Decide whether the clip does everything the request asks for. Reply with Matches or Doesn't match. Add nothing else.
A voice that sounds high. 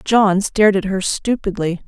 Matches